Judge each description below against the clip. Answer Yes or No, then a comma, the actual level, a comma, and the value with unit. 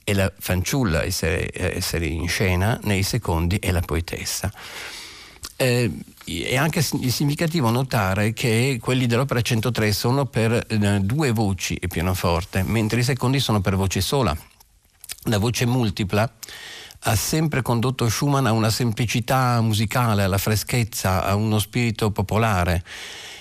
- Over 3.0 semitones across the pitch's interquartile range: Yes, average, 4.3 semitones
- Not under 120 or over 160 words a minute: Yes, average, 125 wpm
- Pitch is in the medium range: No, low, 110 Hz